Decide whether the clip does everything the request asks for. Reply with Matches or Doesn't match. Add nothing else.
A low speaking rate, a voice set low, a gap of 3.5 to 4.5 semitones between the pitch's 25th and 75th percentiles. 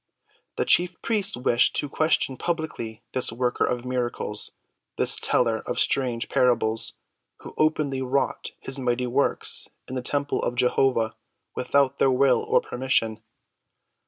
Doesn't match